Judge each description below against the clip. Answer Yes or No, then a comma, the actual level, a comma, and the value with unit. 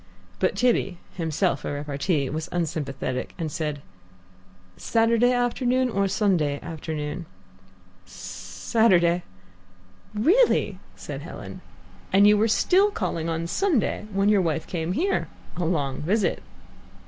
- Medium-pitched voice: Yes, medium, 175 Hz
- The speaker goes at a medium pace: No, slow, 120 wpm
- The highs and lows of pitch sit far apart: Yes, wide, 6.4 semitones